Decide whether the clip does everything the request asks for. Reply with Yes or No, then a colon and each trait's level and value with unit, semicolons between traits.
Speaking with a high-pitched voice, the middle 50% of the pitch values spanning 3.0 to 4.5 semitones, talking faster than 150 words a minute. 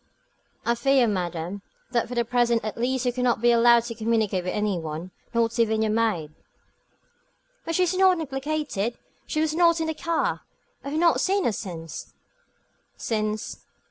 No: high, 235 Hz; average, 5.0 semitones; average, 180 wpm